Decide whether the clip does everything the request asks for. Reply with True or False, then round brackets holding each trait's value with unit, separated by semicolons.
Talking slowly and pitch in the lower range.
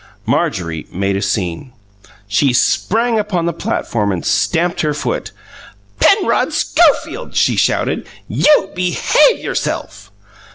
False (115 wpm; 150 Hz)